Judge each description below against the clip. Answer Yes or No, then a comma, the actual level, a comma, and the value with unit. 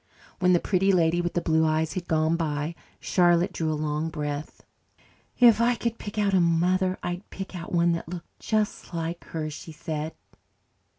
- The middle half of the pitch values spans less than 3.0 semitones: Yes, narrow, 2.6 semitones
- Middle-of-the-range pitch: Yes, medium, 170 Hz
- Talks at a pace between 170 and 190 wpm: Yes, average, 185 wpm